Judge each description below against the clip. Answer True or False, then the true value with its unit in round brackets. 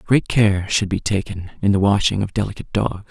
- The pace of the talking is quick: True (215 wpm)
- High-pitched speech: False (100 Hz)